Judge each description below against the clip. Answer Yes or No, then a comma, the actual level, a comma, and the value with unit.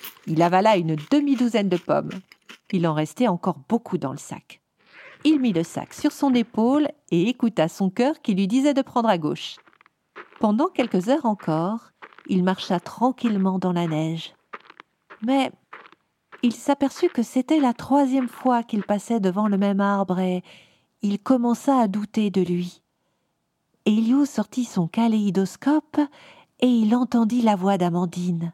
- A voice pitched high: Yes, high, 215 Hz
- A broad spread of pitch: Yes, wide, 5.7 semitones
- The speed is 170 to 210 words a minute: No, average, 155 wpm